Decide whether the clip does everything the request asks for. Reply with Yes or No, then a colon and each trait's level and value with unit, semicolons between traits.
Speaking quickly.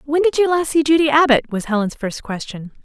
Yes: fast, 230 wpm